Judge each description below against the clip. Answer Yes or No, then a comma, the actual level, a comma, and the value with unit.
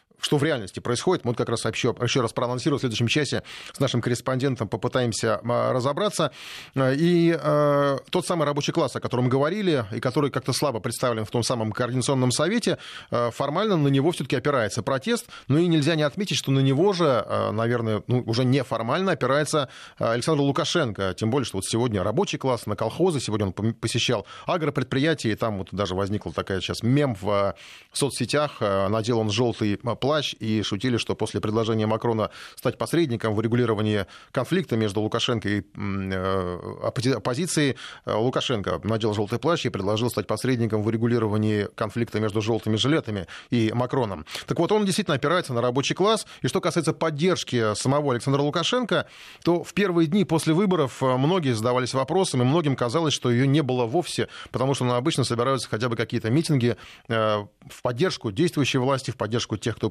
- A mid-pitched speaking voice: No, low, 125 Hz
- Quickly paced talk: Yes, fast, 170 wpm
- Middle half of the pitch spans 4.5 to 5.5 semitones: Yes, average, 4.9 semitones